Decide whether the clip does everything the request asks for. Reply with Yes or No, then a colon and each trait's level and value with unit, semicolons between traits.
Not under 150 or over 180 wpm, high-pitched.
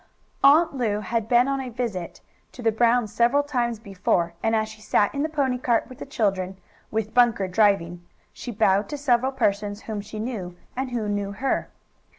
No: average, 190 wpm; high, 225 Hz